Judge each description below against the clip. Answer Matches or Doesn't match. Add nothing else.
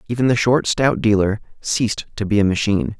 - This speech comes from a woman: Doesn't match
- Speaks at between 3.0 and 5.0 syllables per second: Doesn't match